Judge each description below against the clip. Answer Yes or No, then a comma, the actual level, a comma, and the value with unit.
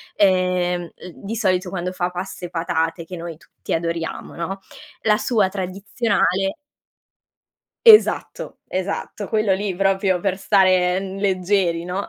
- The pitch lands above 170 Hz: Yes, medium, 185 Hz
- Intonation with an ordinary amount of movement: No, narrow, 1.8 semitones